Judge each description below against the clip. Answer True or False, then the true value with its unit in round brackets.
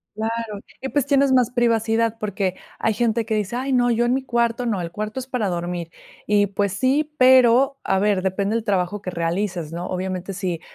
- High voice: True (215 Hz)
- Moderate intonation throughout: True (4.3 semitones)